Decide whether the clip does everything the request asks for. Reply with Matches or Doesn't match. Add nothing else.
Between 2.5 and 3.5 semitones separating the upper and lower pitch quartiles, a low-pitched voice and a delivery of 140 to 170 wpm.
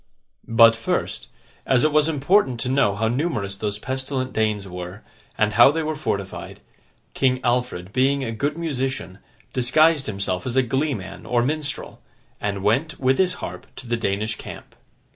Doesn't match